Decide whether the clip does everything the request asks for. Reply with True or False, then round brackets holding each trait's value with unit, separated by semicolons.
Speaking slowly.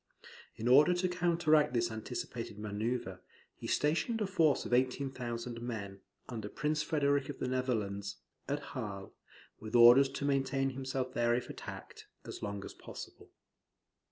False (145 wpm)